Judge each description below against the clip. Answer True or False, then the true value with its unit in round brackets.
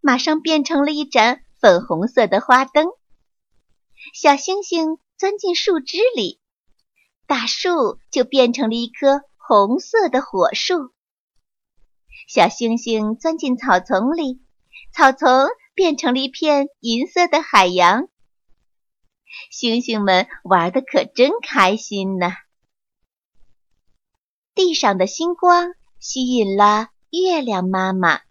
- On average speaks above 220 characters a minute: False (160 characters per minute)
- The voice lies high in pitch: True (265 Hz)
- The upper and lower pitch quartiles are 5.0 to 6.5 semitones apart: False (6.9 semitones)